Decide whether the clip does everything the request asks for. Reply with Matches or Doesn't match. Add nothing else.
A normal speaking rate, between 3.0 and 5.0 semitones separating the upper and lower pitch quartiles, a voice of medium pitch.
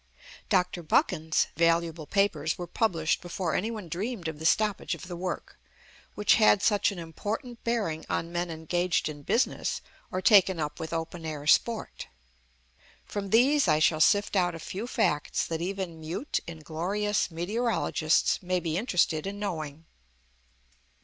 Matches